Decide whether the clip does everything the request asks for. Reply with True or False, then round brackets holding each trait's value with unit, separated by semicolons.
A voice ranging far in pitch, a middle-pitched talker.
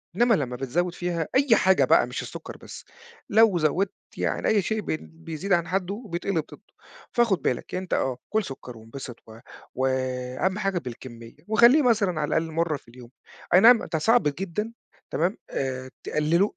True (6.7 semitones; 175 Hz)